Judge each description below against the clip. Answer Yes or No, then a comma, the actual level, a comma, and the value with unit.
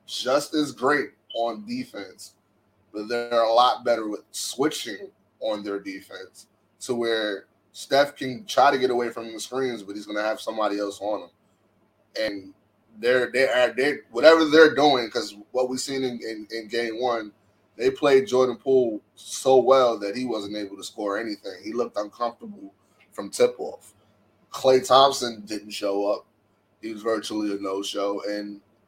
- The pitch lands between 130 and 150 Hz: No, low, 115 Hz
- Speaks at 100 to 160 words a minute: No, average, 170 wpm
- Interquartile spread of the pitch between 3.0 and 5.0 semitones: Yes, average, 4.0 semitones